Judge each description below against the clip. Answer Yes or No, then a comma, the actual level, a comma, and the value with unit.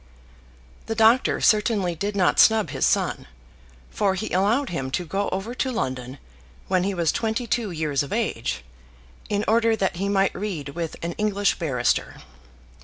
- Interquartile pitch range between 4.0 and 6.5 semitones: Yes, average, 4.5 semitones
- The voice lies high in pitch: Yes, high, 195 Hz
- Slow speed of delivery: No, average, 165 wpm